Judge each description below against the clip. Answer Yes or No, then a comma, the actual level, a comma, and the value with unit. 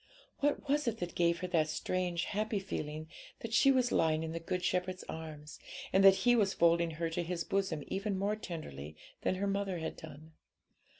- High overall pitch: No, medium, 180 Hz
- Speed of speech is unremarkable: Yes, average, 195 wpm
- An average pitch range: Yes, average, 3.5 semitones